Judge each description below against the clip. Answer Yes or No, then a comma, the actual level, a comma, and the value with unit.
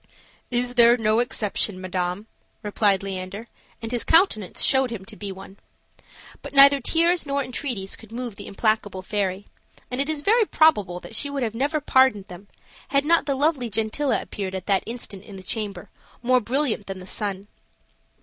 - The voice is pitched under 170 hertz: No, high, 225 Hz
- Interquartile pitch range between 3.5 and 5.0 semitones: No, wide, 5.4 semitones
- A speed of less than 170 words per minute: No, average, 180 wpm